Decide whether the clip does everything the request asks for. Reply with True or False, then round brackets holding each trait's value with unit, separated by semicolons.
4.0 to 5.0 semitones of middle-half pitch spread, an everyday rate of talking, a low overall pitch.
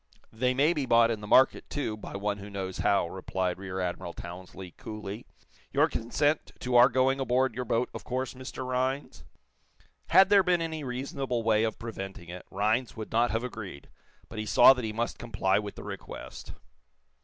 True (4.5 semitones; 190 wpm; 115 Hz)